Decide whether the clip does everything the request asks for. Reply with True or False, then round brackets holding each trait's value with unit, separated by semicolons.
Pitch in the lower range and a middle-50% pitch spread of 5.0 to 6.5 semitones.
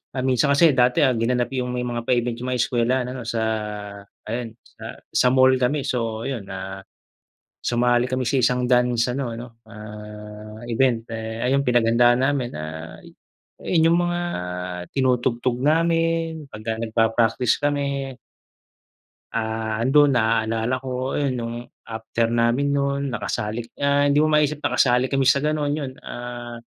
False (125 Hz; 3.0 semitones)